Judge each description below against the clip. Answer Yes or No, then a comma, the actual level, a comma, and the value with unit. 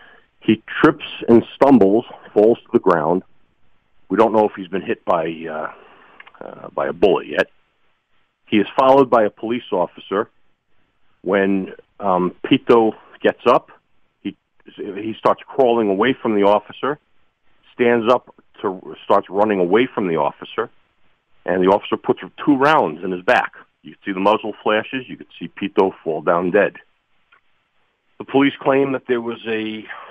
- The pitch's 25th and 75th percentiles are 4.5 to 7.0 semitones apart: No, average, 3.9 semitones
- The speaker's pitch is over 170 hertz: No, low, 110 Hz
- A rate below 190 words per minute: Yes, average, 155 wpm